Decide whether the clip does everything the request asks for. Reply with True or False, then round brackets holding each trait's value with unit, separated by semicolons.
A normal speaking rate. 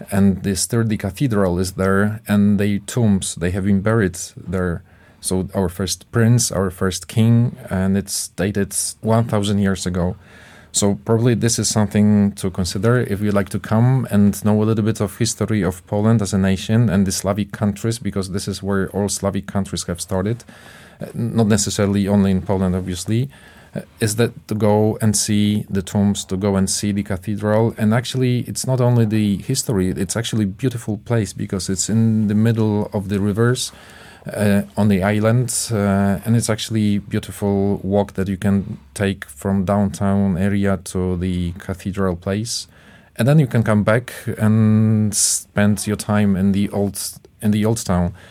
True (180 wpm)